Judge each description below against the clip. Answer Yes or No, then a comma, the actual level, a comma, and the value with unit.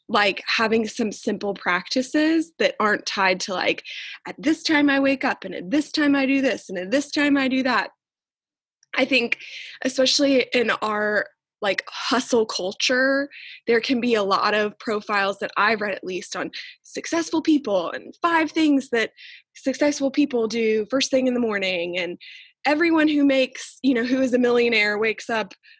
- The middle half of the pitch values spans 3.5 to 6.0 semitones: Yes, average, 5.2 semitones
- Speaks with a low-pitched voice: No, very high, 260 Hz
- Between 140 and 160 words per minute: No, average, 180 wpm